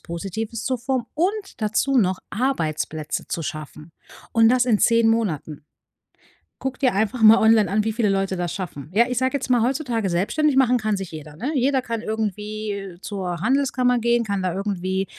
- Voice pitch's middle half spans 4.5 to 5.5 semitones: Yes, average, 4.8 semitones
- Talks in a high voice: Yes, high, 220 Hz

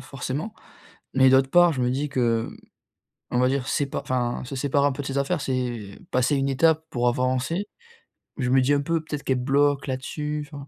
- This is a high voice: No, low, 135 Hz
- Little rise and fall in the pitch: Yes, narrow, 2.2 semitones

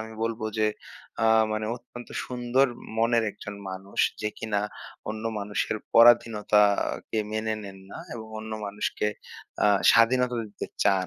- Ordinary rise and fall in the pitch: No, narrow, 2.0 semitones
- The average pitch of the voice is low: Yes, low, 110 Hz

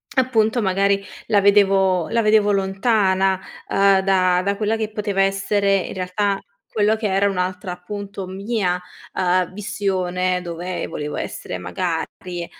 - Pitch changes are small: Yes, narrow, 2.0 semitones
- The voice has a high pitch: Yes, high, 195 Hz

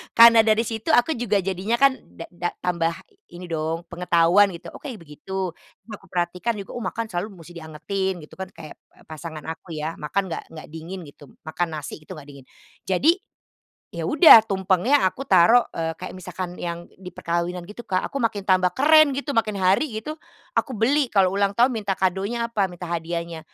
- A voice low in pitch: No, medium, 185 Hz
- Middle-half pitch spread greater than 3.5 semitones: Yes, average, 4.7 semitones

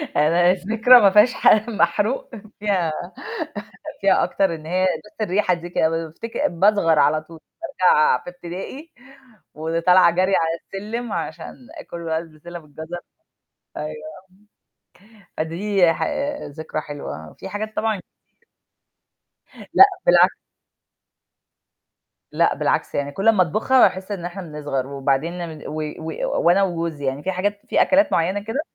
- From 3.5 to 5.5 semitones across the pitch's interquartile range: Yes, average, 4.2 semitones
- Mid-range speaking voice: Yes, medium, 175 Hz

